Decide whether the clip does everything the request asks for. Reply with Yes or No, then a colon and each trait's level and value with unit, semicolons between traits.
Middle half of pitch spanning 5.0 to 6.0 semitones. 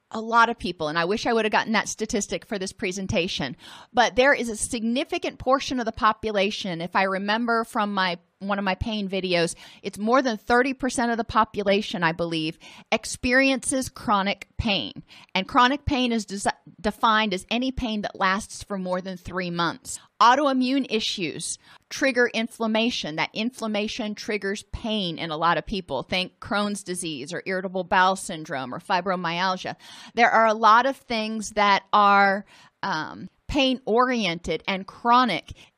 No: average, 3.8 semitones